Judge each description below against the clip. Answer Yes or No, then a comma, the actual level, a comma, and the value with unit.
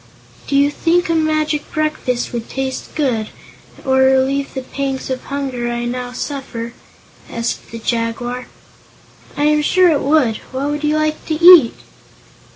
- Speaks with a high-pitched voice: Yes, very high, 270 Hz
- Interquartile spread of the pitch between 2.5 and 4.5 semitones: Yes, average, 3.6 semitones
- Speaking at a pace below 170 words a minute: Yes, average, 155 wpm